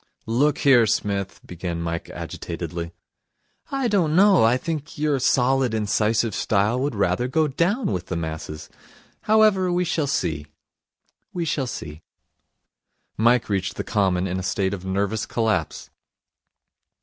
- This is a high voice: No, low, 110 Hz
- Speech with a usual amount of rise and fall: No, wide, 8.0 semitones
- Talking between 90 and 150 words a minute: Yes, average, 140 wpm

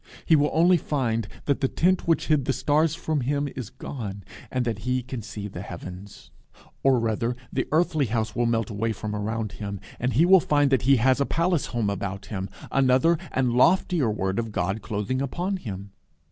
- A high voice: No, low, 125 Hz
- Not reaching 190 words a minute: No, average, 200 wpm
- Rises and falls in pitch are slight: No, wide, 5.6 semitones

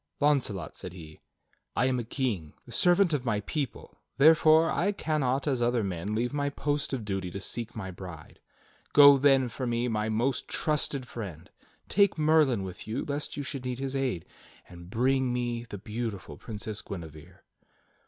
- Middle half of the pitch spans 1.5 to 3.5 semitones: No, wide, 5.5 semitones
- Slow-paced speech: No, average, 175 wpm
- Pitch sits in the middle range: No, low, 120 Hz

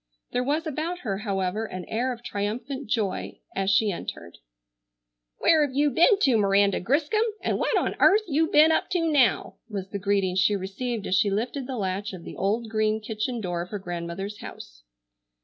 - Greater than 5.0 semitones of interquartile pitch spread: Yes, wide, 5.5 semitones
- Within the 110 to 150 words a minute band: No, average, 190 wpm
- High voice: Yes, high, 215 Hz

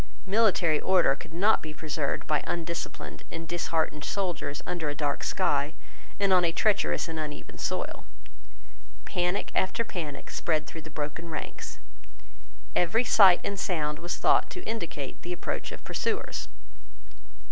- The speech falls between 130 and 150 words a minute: Yes, average, 145 wpm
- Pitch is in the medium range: Yes, medium, 165 Hz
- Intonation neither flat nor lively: Yes, average, 3.7 semitones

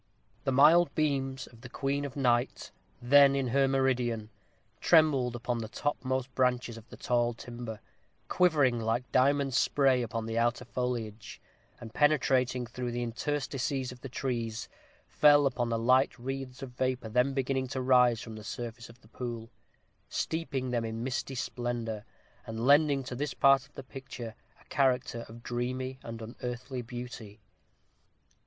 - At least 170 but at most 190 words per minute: No, average, 155 wpm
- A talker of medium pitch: No, low, 125 Hz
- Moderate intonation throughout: No, narrow, 2.2 semitones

